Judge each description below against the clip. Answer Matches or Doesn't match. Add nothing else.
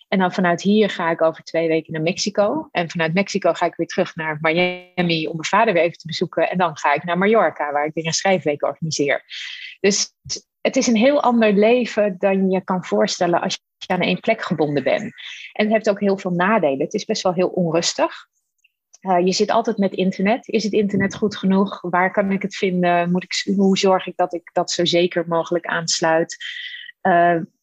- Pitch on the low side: Doesn't match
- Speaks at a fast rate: Matches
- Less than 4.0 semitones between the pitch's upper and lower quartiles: Matches